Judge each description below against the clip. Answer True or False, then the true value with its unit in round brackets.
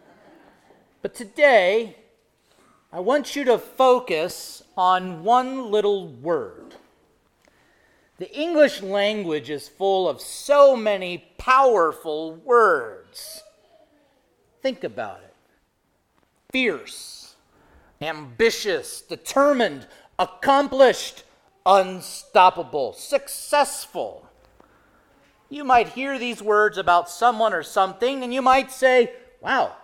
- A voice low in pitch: False (255 Hz)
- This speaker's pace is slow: True (90 wpm)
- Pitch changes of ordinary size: False (6.6 semitones)